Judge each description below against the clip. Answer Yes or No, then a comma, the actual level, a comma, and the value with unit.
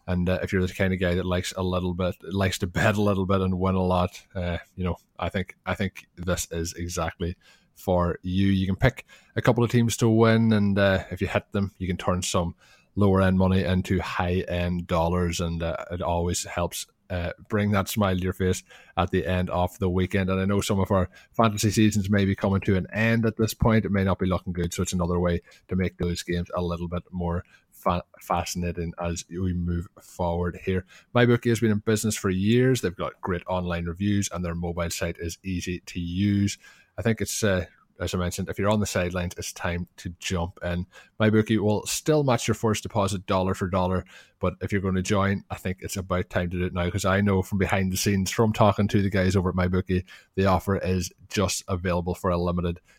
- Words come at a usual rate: No, fast, 230 wpm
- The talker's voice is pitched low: Yes, very low, 95 Hz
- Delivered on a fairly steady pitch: Yes, narrow, 2.2 semitones